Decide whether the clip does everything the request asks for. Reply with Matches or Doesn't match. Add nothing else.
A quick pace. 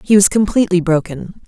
Doesn't match